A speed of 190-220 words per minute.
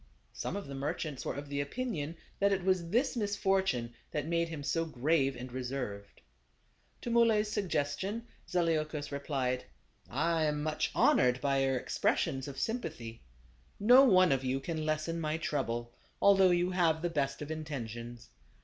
No: average, 160 wpm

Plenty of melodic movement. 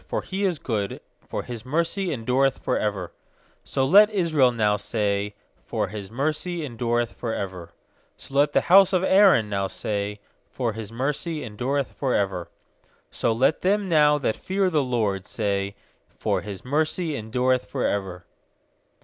Yes: wide, 6.9 semitones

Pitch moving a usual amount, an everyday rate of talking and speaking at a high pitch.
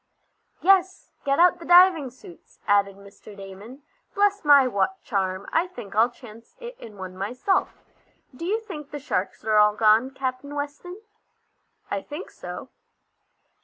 No: wide, 9.0 semitones; average, 150 wpm; very high, 260 Hz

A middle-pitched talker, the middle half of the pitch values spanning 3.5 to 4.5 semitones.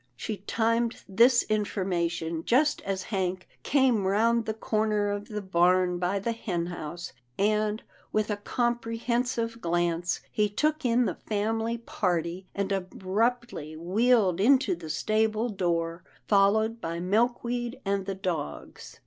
No: high, 205 Hz; average, 4.2 semitones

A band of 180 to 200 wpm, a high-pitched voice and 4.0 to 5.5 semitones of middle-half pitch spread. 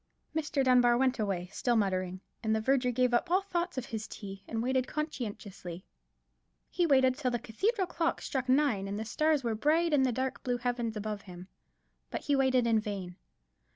Yes: average, 190 wpm; high, 245 Hz; average, 4.3 semitones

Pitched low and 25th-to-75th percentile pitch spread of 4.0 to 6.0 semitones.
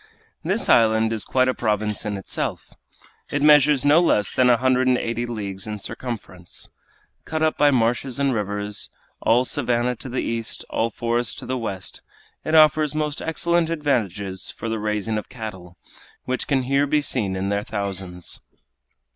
Yes: low, 120 Hz; average, 4.8 semitones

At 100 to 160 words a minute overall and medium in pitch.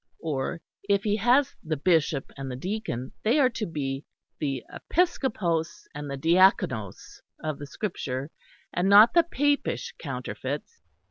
Yes: average, 140 wpm; medium, 170 Hz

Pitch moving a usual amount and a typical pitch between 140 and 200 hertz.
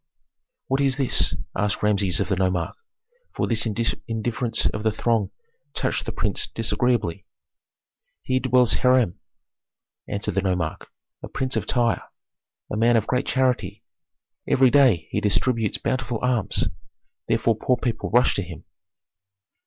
No: average, 3.9 semitones; low, 115 Hz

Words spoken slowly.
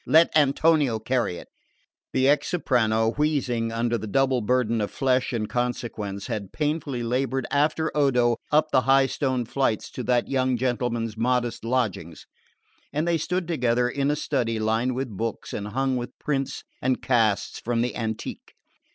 No: average, 160 wpm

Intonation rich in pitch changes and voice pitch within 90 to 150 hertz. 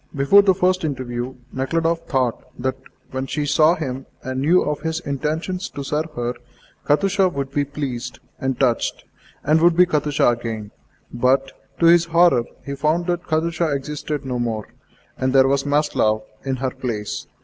No: average, 4.0 semitones; medium, 140 Hz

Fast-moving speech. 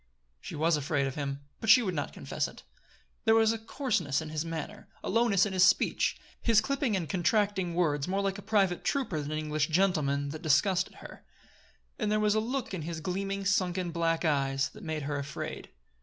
Yes: fast, 210 wpm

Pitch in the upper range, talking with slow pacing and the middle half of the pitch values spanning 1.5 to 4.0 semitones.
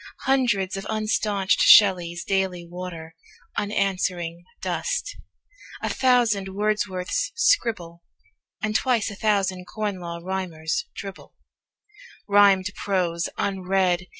Yes: high, 195 Hz; slow, 95 wpm; average, 2.8 semitones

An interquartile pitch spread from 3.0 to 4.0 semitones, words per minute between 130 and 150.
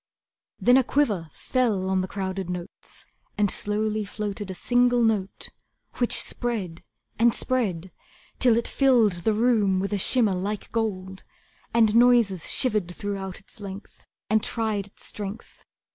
Yes: average, 3.5 semitones; average, 145 wpm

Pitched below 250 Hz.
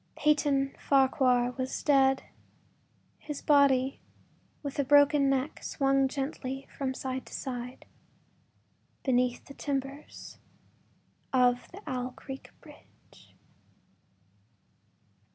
No: very high, 270 Hz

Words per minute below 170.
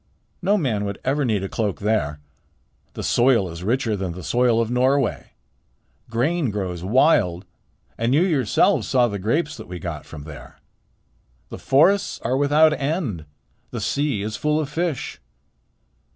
Yes: average, 155 wpm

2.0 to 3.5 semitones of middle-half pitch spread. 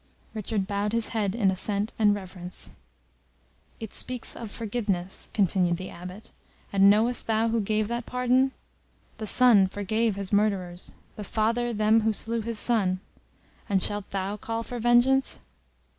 Yes: average, 2.8 semitones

